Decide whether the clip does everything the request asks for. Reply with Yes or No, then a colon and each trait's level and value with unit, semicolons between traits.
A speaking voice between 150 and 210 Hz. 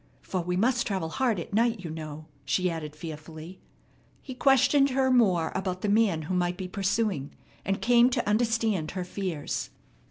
Yes: high, 190 Hz